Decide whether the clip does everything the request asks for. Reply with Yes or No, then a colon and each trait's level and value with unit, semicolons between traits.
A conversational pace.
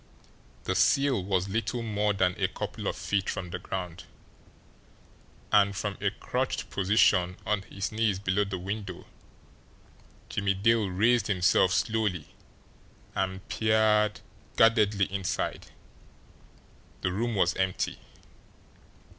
No: slow, 115 wpm